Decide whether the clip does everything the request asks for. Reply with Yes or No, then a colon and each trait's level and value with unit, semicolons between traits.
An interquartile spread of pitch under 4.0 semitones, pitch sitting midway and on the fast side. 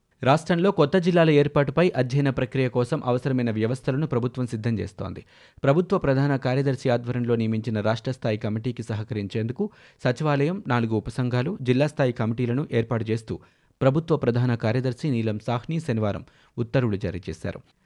No: average, 3.4 semitones; low, 125 Hz; fast, 130 wpm